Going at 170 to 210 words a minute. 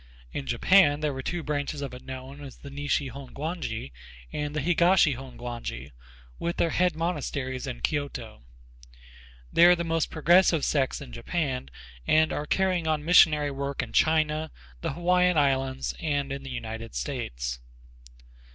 No: average, 150 wpm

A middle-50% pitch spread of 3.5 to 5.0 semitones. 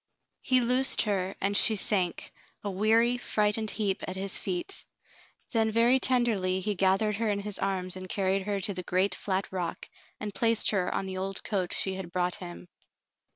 No: average, 2.8 semitones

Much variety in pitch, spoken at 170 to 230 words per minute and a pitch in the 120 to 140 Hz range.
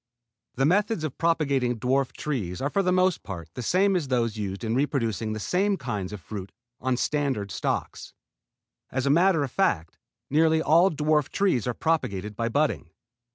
Yes: wide, 6.6 semitones; average, 175 wpm; low, 135 Hz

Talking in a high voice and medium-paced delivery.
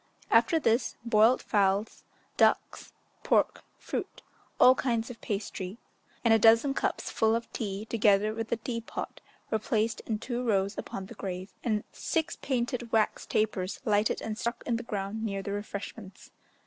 Yes: high, 220 Hz; average, 160 wpm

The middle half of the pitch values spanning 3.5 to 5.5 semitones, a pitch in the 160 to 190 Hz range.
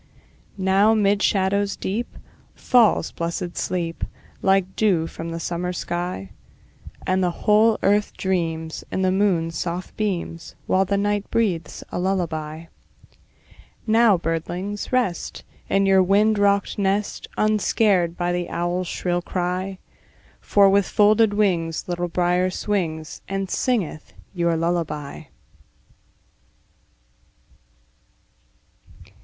No: average, 2.9 semitones; medium, 185 Hz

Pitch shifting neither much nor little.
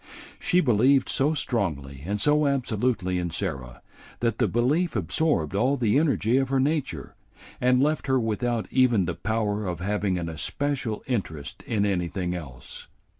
No: wide, 6.6 semitones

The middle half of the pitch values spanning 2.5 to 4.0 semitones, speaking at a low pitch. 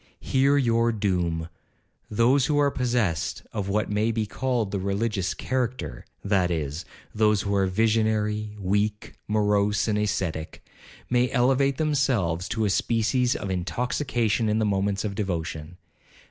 Yes: average, 3.7 semitones; low, 105 Hz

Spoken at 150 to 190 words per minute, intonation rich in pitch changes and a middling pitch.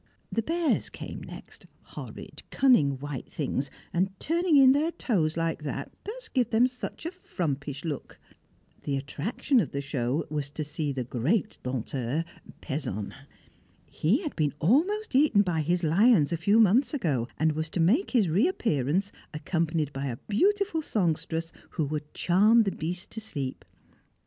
Yes: average, 160 wpm; wide, 8.5 semitones; medium, 165 Hz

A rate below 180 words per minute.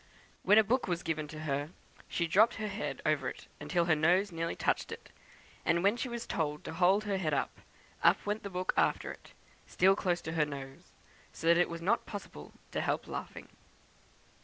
No: average, 200 wpm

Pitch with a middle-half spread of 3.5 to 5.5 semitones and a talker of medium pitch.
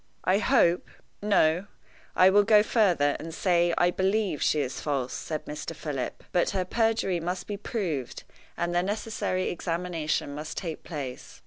Yes: average, 4.3 semitones; medium, 175 Hz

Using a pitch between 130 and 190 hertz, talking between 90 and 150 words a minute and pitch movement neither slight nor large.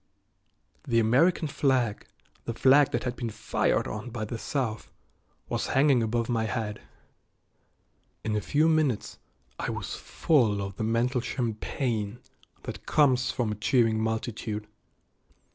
No: low, 115 Hz; slow, 135 wpm; average, 3.1 semitones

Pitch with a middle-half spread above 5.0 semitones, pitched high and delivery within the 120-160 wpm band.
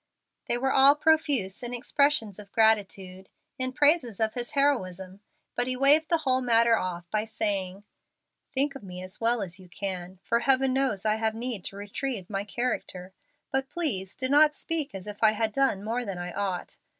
No: wide, 5.6 semitones; high, 225 Hz; average, 190 wpm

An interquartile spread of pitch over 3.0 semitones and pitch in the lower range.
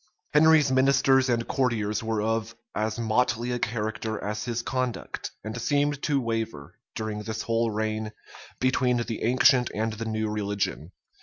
No: narrow, 2.6 semitones; low, 115 Hz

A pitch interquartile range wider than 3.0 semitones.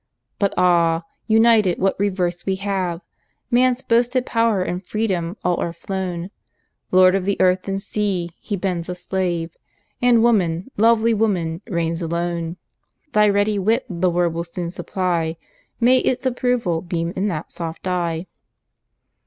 Yes: average, 3.6 semitones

